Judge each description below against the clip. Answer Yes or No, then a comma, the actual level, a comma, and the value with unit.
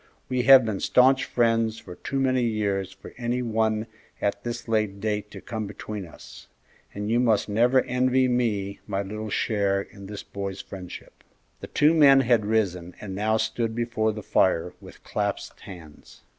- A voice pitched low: Yes, low, 110 Hz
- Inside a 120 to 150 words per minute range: No, average, 170 wpm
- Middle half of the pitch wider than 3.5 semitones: No, average, 3.2 semitones